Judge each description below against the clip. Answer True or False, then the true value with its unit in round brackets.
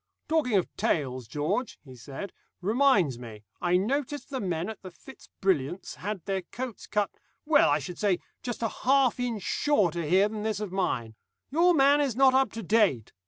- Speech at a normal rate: True (185 wpm)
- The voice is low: False (205 Hz)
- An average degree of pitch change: False (7.1 semitones)